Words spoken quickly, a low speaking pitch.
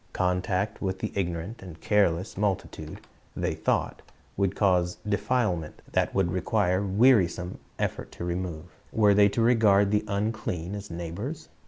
No: average, 140 wpm; very low, 95 Hz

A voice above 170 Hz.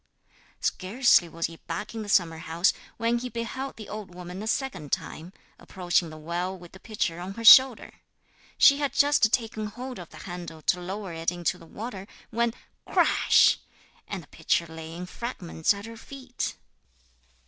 Yes: high, 190 Hz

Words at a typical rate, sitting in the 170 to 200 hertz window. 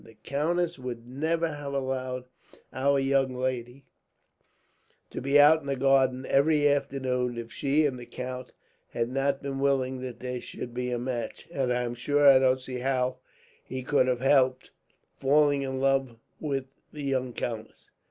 No: average, 165 wpm; low, 130 Hz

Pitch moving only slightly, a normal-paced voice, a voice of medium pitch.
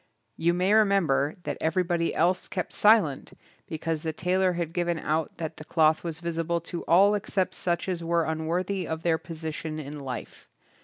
Yes: narrow, 2.2 semitones; average, 170 wpm; medium, 170 Hz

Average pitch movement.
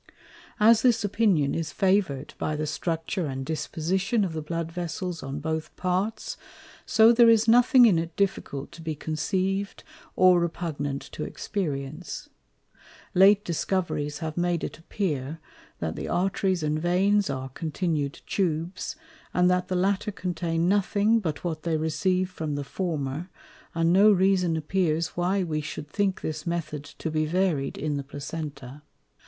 Yes: average, 3.8 semitones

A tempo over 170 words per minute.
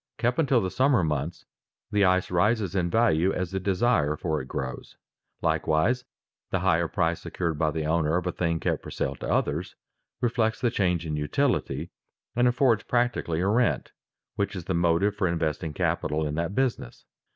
Yes: average, 180 wpm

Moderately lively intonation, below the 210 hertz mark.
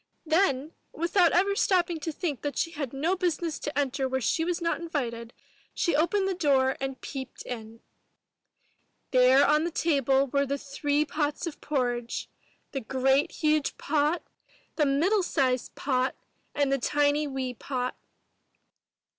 No: average, 3.7 semitones; very high, 285 Hz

